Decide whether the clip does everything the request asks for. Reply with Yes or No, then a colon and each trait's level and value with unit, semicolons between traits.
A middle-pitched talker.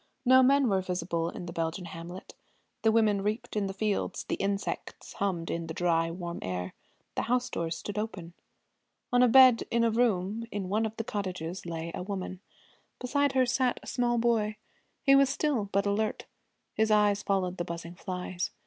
No: high, 200 Hz